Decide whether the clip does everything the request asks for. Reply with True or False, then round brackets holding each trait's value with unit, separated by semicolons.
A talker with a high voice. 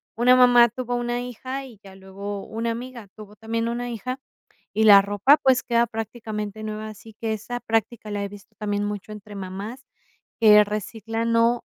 True (220 Hz)